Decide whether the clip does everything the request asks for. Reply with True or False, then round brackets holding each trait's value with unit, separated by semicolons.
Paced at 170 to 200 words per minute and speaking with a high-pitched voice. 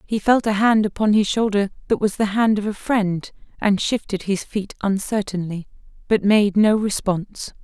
True (180 wpm; 205 Hz)